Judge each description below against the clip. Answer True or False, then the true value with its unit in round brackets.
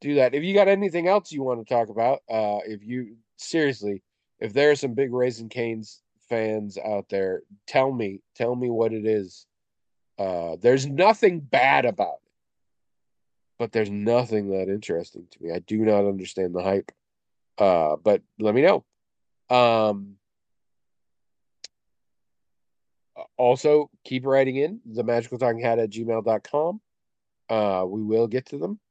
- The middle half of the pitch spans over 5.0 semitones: False (4.4 semitones)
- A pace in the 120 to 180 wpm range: True (155 wpm)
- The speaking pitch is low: True (115 Hz)